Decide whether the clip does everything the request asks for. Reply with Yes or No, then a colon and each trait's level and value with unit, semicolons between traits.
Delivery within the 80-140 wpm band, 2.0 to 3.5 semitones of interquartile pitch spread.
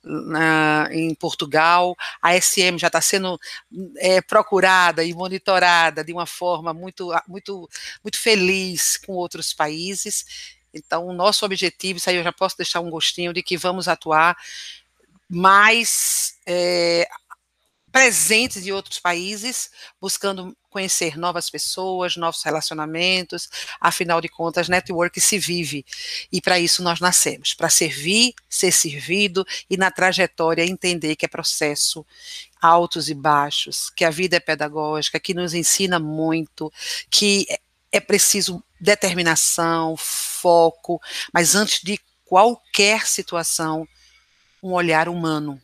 Yes: average, 130 wpm; narrow, 2.5 semitones